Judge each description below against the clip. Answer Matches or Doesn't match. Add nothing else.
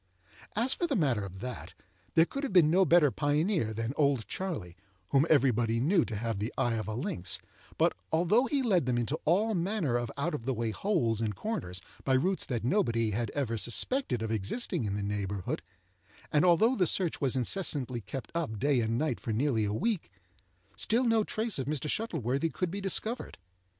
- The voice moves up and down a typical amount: Doesn't match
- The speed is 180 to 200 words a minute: Matches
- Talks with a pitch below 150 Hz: Matches